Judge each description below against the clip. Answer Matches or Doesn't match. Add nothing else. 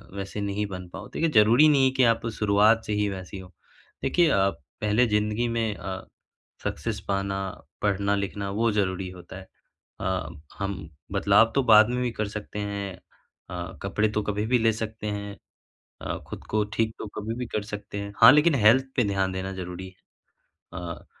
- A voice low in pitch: Matches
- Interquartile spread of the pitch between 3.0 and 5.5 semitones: Doesn't match